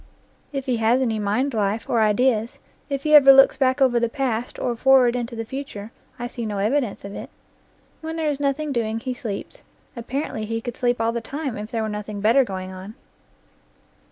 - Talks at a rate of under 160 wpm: No, fast, 205 wpm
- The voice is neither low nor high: No, high, 235 Hz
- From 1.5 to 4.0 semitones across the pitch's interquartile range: Yes, average, 3.6 semitones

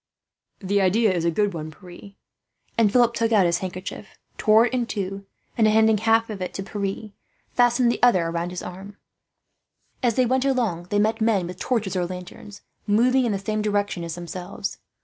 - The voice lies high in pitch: Yes, high, 205 Hz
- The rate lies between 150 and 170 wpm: No, average, 190 wpm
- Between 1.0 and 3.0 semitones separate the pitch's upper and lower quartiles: No, average, 3.7 semitones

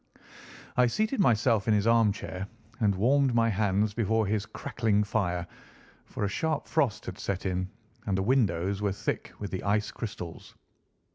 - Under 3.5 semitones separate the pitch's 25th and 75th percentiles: Yes, average, 2.9 semitones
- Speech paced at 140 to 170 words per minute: Yes, average, 160 wpm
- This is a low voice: Yes, low, 105 Hz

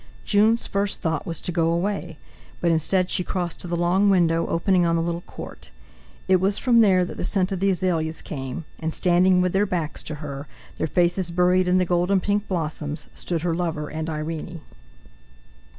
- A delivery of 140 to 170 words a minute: No, average, 195 wpm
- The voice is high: No, medium, 175 Hz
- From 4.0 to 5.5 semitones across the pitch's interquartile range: No, narrow, 2.4 semitones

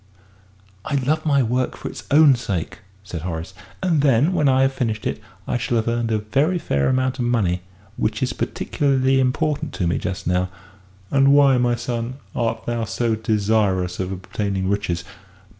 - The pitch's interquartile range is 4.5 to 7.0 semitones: Yes, average, 5.0 semitones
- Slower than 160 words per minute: No, average, 175 wpm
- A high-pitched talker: No, low, 120 Hz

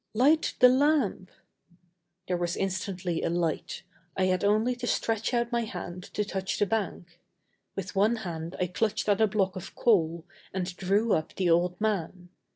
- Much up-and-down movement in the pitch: No, average, 3.7 semitones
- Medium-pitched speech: No, high, 195 Hz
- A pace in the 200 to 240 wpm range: No, average, 170 wpm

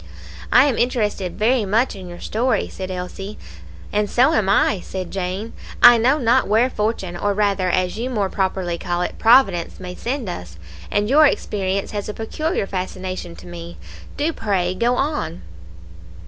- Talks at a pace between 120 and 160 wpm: No, average, 170 wpm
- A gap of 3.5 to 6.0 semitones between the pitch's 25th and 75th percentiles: Yes, average, 4.3 semitones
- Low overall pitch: No, high, 205 Hz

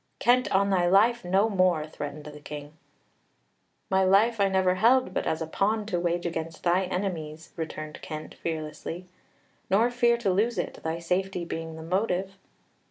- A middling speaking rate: Yes, average, 165 wpm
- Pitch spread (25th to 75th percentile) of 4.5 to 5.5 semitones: No, average, 3.5 semitones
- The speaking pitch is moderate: Yes, medium, 180 Hz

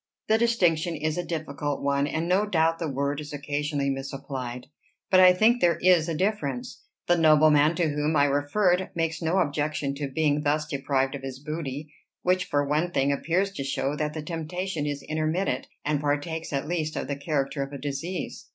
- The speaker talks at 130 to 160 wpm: No, average, 190 wpm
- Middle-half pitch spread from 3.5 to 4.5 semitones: No, average, 3.0 semitones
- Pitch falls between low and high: Yes, medium, 150 Hz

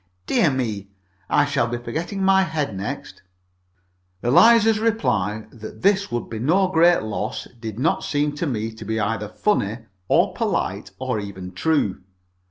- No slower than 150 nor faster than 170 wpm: Yes, average, 155 wpm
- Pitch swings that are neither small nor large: No, wide, 7.9 semitones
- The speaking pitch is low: Yes, low, 120 Hz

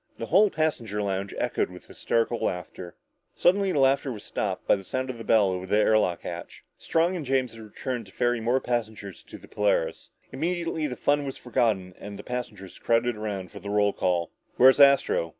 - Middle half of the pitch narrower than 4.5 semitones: No, average, 5.1 semitones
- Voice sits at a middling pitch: No, low, 115 Hz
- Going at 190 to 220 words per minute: Yes, fast, 205 wpm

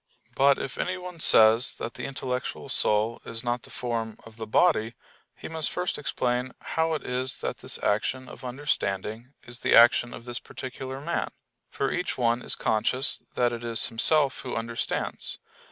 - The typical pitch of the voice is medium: No, low, 125 Hz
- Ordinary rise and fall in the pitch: Yes, average, 3.0 semitones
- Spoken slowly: No, average, 170 wpm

